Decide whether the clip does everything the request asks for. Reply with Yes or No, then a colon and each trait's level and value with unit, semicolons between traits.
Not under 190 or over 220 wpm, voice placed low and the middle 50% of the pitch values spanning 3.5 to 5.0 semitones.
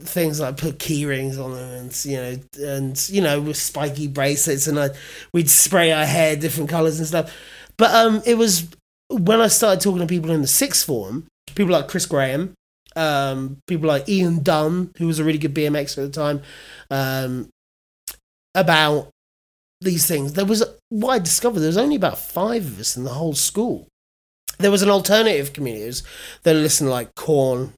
No: average, 195 wpm; medium, 155 Hz; average, 4.5 semitones